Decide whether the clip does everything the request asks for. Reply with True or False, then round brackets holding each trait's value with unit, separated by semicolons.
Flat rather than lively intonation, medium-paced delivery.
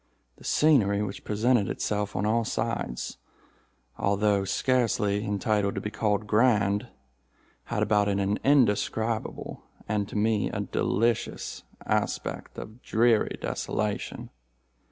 False (1.9 semitones; 115 wpm)